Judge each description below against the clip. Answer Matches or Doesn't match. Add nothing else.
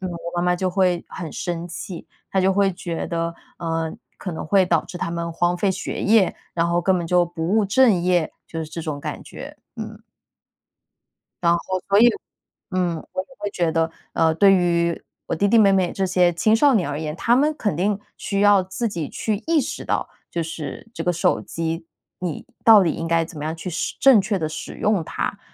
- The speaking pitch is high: Doesn't match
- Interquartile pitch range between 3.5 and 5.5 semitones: Doesn't match